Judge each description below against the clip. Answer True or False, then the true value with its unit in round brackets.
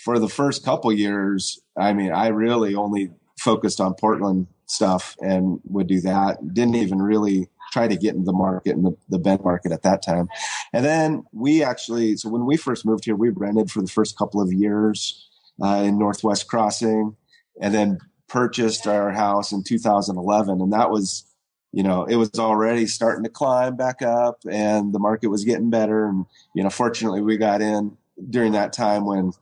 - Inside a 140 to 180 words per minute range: False (190 wpm)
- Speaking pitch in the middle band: False (105 Hz)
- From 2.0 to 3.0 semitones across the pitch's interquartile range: True (2.5 semitones)